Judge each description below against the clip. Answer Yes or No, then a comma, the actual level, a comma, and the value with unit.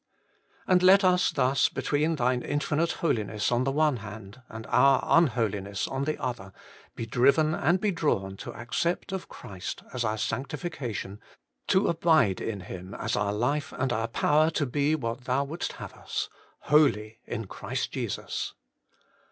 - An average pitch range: No, wide, 6.0 semitones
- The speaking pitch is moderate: No, low, 130 Hz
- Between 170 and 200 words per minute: No, average, 160 wpm